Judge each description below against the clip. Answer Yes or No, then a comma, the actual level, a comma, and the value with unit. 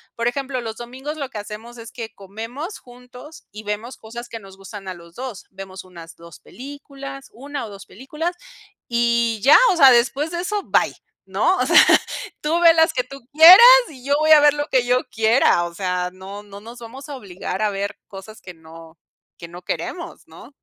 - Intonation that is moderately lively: No, wide, 5.8 semitones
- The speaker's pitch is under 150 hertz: No, high, 235 Hz